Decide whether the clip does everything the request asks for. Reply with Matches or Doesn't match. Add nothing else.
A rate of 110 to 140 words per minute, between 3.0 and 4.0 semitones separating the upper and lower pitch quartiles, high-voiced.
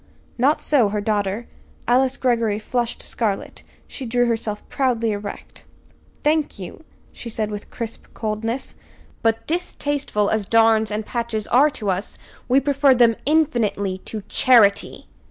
Matches